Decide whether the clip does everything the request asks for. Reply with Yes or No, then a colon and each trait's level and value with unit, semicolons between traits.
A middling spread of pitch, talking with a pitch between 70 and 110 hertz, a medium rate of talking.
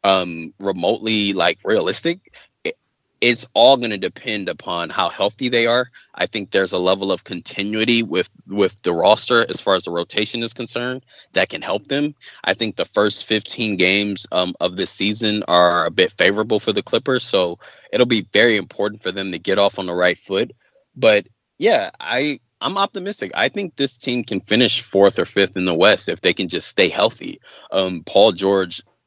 Yes: average, 4.2 semitones; low, 105 Hz; average, 195 wpm